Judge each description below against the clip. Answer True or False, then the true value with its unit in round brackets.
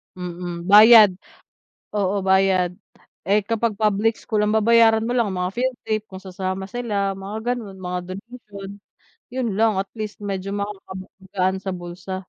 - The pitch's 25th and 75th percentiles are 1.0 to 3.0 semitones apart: True (2.7 semitones)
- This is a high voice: True (200 Hz)